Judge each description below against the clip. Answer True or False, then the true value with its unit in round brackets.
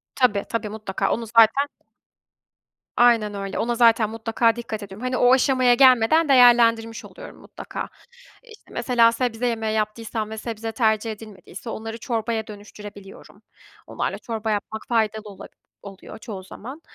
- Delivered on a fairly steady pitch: True (2.1 semitones)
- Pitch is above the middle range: True (225 Hz)